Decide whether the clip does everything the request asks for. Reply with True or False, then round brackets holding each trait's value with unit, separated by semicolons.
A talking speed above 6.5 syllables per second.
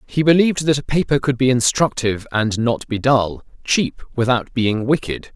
False (5.0 syllables/s)